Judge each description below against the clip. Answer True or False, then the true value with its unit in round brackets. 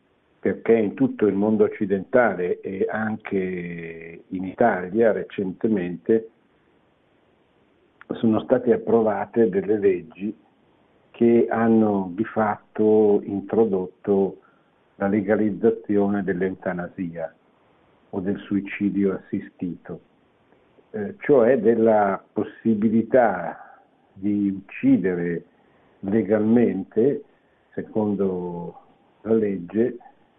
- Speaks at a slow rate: True (75 wpm)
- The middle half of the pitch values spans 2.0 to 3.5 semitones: True (2.8 semitones)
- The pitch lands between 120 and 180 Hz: False (105 Hz)